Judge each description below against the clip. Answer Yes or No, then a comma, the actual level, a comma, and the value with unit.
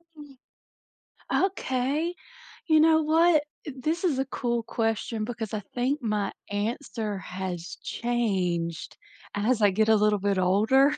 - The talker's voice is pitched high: Yes, high, 230 Hz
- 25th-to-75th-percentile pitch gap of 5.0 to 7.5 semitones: Yes, wide, 5.4 semitones